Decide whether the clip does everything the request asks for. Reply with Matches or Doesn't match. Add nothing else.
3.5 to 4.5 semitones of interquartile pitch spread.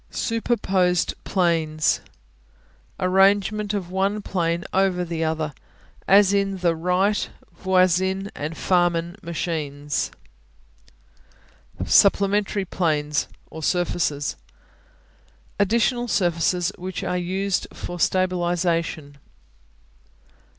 Doesn't match